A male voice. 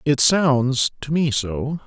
Yes: male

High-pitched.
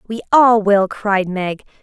Yes: high, 205 Hz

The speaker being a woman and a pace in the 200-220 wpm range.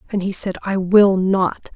Yes: female; fast, 205 wpm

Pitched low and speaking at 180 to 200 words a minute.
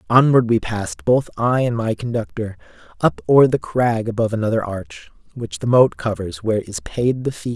Yes: low, 115 Hz; average, 190 wpm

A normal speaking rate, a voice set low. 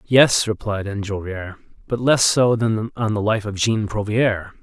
Yes: average, 170 wpm; low, 110 Hz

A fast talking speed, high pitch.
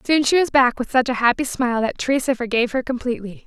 Yes: fast, 245 wpm; very high, 250 Hz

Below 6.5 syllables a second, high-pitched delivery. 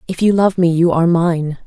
No: 5.5 syllables/s; medium, 170 Hz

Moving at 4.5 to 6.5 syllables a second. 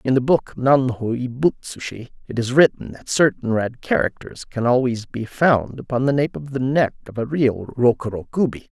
Yes: 4.9 syllables/s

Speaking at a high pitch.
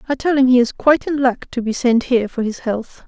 Yes: very high, 250 Hz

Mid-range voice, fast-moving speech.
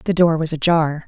Yes: medium, 160 Hz; fast, 225 wpm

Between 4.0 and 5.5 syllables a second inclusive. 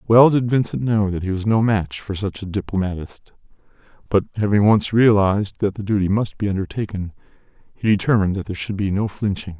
No: 6.0 syllables/s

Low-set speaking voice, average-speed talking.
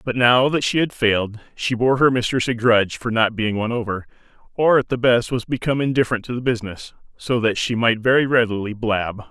No: low, 120 Hz; fast, 220 wpm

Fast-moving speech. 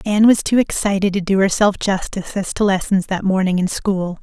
Yes: fast, 215 wpm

